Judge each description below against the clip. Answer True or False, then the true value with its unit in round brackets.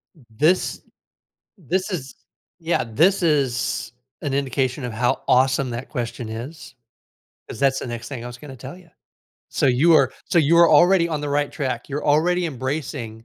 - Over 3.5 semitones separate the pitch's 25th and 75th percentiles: True (4.5 semitones)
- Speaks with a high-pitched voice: False (140 Hz)